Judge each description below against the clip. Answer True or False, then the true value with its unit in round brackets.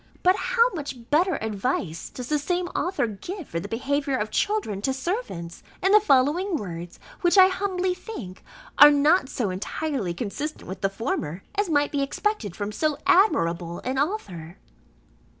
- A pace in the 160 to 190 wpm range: True (165 wpm)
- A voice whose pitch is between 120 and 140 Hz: False (280 Hz)